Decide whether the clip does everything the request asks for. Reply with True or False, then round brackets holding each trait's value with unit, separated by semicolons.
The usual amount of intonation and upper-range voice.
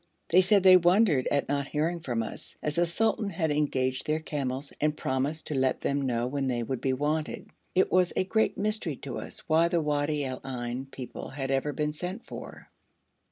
False (4.3 semitones; 150 Hz)